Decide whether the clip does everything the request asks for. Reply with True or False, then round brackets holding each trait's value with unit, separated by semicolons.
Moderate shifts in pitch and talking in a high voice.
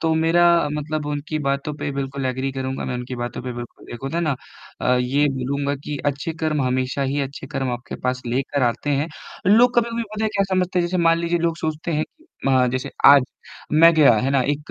False (3.8 semitones; 145 Hz)